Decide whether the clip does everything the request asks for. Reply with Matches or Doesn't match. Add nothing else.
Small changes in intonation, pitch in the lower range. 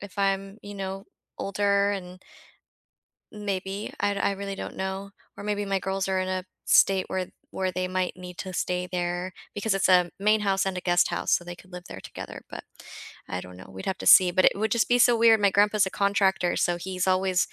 Doesn't match